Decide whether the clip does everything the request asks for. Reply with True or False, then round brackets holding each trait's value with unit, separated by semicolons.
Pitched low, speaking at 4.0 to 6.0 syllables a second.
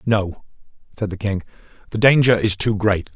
True (105 Hz; 5.0 syllables/s)